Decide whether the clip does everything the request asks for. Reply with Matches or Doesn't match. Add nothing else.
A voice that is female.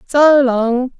Matches